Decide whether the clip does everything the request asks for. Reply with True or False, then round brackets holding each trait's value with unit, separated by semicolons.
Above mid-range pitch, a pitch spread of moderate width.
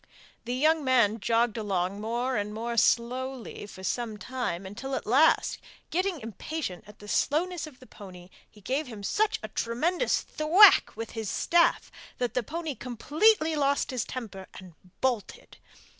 False (245 Hz; 6.3 semitones)